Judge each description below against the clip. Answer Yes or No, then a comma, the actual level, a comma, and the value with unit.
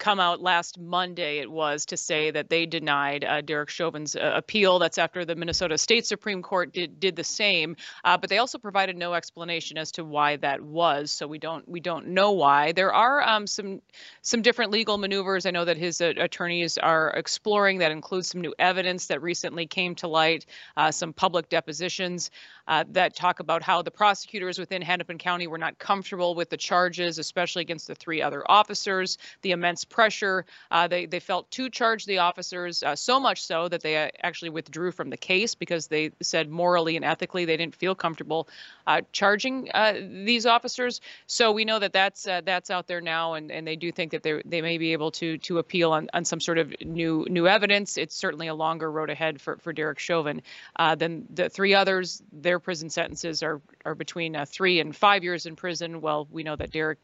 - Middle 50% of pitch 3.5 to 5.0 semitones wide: No, narrow, 2.6 semitones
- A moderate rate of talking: No, fast, 210 wpm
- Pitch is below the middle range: No, medium, 175 Hz